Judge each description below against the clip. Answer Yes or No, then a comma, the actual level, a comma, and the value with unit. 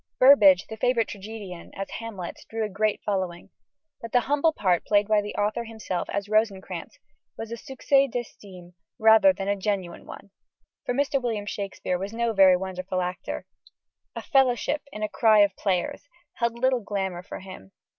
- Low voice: No, high, 210 Hz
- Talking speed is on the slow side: No, average, 170 wpm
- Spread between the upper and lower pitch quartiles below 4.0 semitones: Yes, average, 3.5 semitones